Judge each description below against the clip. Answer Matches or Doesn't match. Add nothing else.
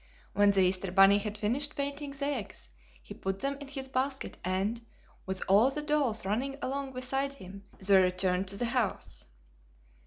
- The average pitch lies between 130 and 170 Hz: Doesn't match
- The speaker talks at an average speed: Matches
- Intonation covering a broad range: Matches